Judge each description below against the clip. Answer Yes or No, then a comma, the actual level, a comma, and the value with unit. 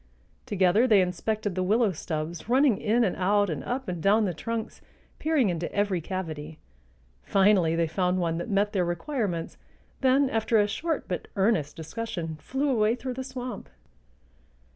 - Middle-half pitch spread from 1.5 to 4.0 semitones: No, average, 4.9 semitones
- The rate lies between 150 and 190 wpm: Yes, average, 165 wpm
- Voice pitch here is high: Yes, high, 200 Hz